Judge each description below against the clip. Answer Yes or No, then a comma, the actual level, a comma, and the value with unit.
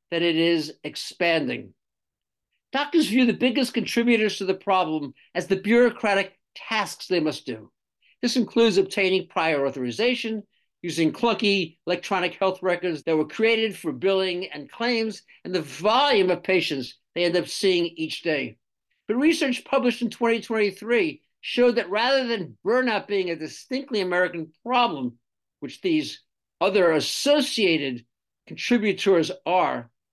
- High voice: Yes, high, 195 Hz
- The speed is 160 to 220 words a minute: No, slow, 135 wpm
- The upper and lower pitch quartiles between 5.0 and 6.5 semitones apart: Yes, wide, 5.6 semitones